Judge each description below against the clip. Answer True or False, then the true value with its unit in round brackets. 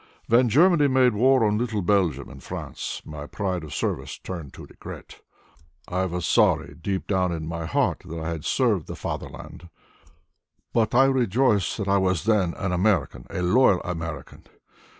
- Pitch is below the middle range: True (95 Hz)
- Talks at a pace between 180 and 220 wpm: False (170 wpm)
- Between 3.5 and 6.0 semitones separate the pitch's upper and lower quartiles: True (5.4 semitones)